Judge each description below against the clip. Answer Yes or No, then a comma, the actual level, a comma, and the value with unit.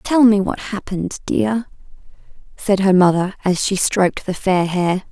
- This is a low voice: No, high, 195 Hz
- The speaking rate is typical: Yes, average, 165 wpm